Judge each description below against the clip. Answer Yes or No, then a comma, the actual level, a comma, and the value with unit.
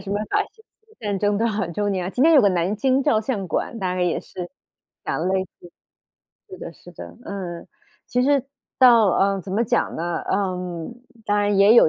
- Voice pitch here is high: Yes, high, 205 Hz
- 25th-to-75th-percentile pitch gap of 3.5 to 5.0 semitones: Yes, average, 4.2 semitones